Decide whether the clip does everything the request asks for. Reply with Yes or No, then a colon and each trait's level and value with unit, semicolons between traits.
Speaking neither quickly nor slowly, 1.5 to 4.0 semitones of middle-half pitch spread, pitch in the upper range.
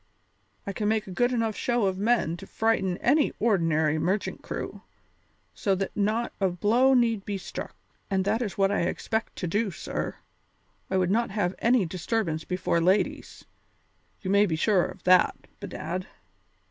Yes: average, 170 wpm; average, 3.5 semitones; high, 200 Hz